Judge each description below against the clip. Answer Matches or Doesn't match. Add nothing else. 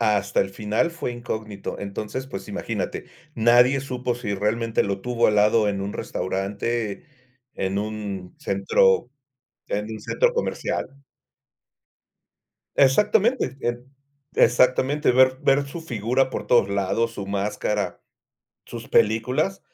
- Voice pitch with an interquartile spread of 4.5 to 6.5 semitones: Doesn't match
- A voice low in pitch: Matches